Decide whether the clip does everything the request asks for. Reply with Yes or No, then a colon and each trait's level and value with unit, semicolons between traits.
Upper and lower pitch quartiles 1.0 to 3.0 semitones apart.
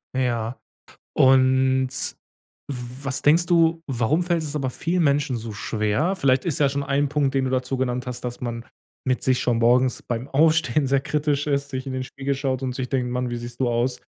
Yes: narrow, 2.4 semitones